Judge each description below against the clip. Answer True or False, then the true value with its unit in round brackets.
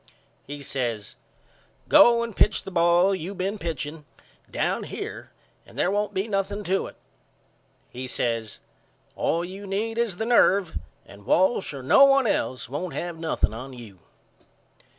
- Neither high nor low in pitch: True (175 Hz)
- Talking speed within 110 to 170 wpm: True (150 wpm)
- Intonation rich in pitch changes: True (6.8 semitones)